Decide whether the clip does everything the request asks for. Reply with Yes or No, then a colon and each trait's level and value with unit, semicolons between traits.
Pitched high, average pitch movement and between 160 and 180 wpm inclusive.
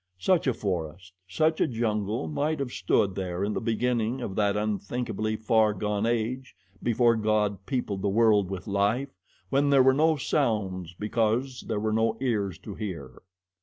No: low, 110 Hz; average, 3.6 semitones; average, 165 wpm